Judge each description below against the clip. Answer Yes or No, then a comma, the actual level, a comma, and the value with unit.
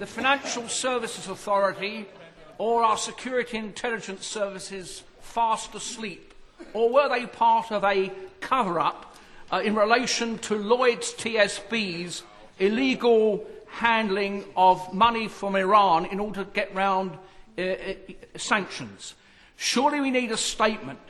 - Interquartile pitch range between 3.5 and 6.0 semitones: No, average, 3.1 semitones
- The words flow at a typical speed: No, slow, 120 wpm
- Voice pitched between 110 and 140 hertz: No, high, 215 Hz